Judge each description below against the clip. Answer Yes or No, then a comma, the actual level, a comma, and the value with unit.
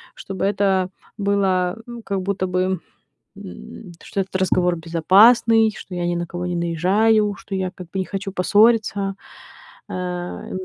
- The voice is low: No, high, 190 Hz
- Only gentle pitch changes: Yes, narrow, 2.1 semitones